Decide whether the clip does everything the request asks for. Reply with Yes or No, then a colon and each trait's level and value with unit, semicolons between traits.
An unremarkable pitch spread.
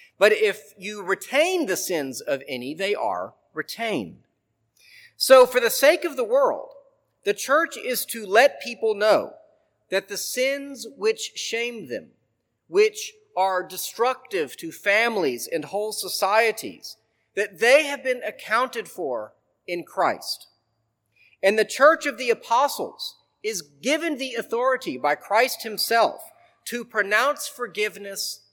No: wide, 7.7 semitones